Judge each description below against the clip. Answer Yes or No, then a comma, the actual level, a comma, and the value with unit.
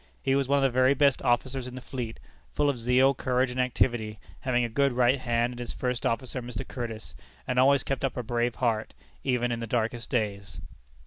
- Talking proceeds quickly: Yes, fast, 215 wpm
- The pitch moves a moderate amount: No, narrow, 1.8 semitones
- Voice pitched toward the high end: No, low, 125 Hz